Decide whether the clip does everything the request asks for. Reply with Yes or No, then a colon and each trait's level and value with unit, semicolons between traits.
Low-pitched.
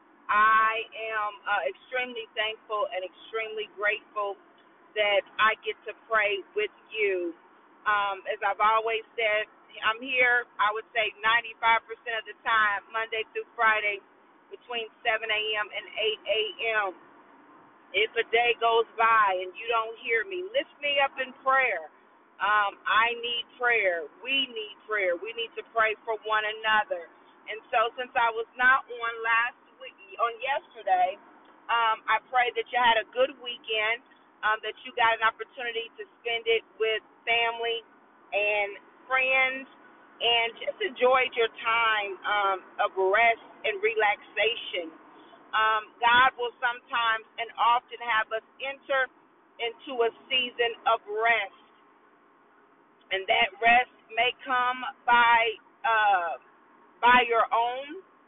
No: high, 230 Hz